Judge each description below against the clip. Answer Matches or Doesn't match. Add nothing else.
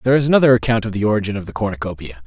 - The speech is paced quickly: Matches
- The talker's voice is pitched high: Doesn't match